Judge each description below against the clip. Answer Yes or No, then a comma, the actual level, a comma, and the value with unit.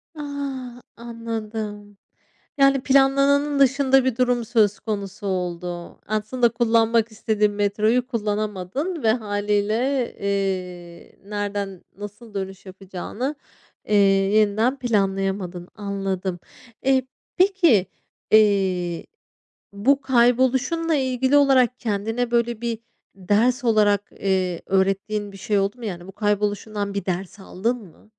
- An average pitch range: Yes, average, 4.0 semitones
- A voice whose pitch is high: Yes, high, 215 Hz